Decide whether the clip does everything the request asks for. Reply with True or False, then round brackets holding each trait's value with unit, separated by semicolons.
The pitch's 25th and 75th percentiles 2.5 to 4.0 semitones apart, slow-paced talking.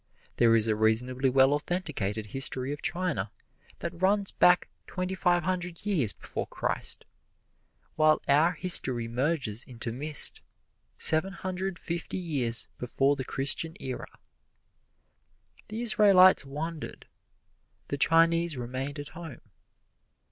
False (5.6 semitones; 120 wpm)